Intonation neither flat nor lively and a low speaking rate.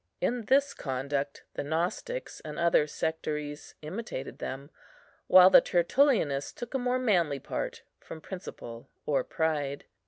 No: wide, 7.4 semitones; slow, 130 wpm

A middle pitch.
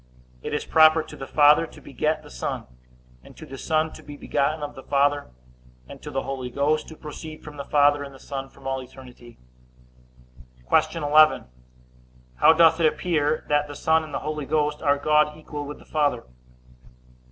Yes: medium, 150 Hz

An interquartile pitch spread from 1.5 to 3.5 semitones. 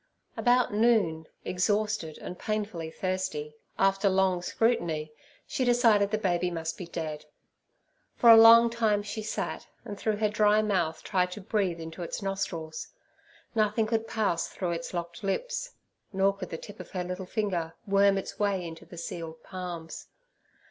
No: average, 3.9 semitones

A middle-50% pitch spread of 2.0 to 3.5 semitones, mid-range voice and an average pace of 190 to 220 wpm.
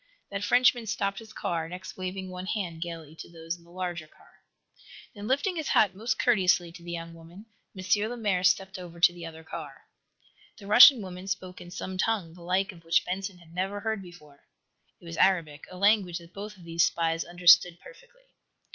Yes: average, 3.1 semitones; medium, 180 Hz; average, 200 wpm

